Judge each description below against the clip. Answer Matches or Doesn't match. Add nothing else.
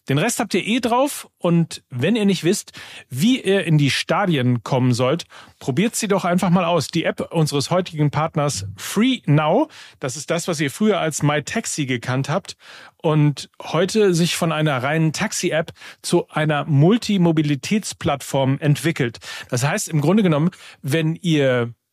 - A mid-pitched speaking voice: Matches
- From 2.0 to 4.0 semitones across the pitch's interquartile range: Doesn't match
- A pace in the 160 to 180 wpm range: Matches